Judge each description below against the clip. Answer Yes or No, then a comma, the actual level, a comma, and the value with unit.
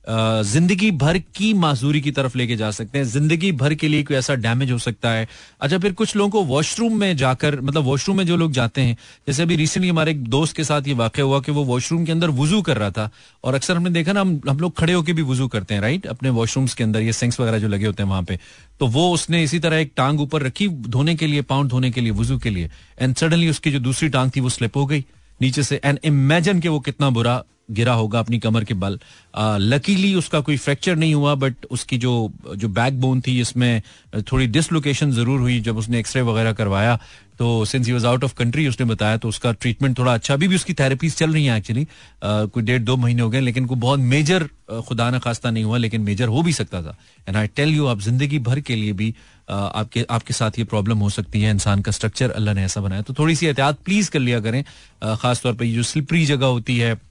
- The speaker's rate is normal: No, fast, 240 wpm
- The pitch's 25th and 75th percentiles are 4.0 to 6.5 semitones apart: Yes, average, 4.7 semitones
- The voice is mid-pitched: No, low, 130 Hz